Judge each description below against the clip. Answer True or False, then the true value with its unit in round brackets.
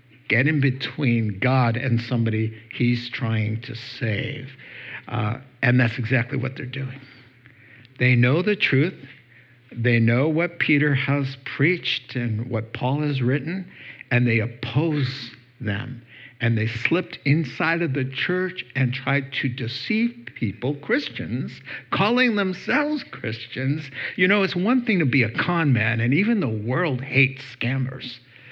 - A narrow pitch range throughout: False (3.4 semitones)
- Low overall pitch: True (130 Hz)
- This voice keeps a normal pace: True (145 wpm)